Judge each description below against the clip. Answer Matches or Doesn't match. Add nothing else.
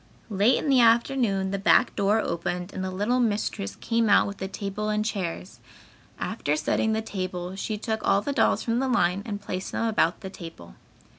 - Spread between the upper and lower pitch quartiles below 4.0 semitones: Matches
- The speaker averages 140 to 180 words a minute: Doesn't match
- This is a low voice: Doesn't match